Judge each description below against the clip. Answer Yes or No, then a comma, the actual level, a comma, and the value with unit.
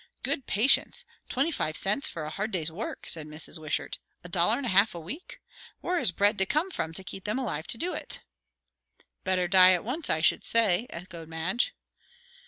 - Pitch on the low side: No, high, 190 Hz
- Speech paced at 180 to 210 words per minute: Yes, average, 200 wpm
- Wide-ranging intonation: Yes, wide, 6.4 semitones